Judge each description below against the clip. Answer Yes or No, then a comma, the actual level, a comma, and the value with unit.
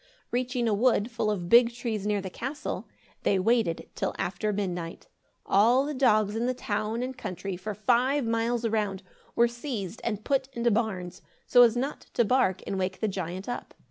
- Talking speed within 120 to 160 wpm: No, average, 185 wpm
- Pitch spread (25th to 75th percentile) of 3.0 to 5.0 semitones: Yes, average, 3.6 semitones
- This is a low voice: No, high, 225 Hz